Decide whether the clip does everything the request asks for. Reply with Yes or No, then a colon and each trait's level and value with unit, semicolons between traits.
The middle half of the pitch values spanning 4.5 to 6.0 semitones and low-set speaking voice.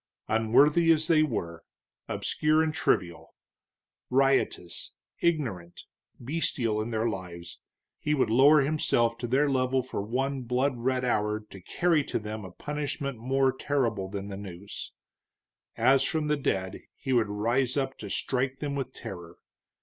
Yes: average, 4.8 semitones; low, 125 Hz